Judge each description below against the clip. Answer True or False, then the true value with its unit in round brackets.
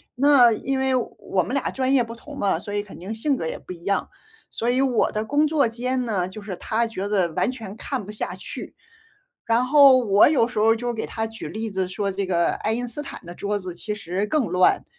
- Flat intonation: False (4.3 semitones)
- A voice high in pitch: True (225 Hz)